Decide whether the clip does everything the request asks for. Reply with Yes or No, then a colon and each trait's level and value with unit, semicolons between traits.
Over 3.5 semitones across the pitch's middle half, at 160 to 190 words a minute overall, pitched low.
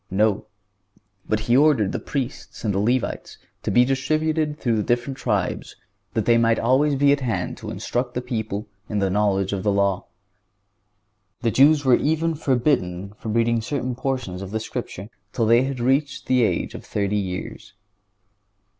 Yes: average, 4.6 semitones; average, 170 wpm; low, 120 Hz